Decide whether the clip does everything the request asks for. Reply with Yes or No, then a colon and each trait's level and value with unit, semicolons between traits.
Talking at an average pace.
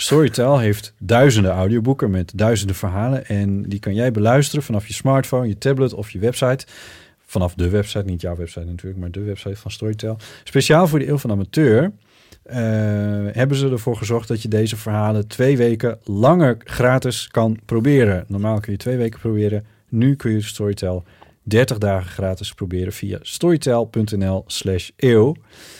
Yes: average, 160 wpm